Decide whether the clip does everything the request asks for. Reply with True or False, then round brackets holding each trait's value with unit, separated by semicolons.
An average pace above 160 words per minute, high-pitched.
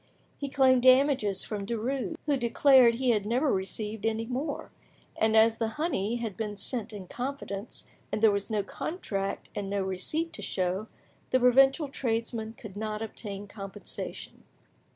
False (155 wpm; 225 Hz)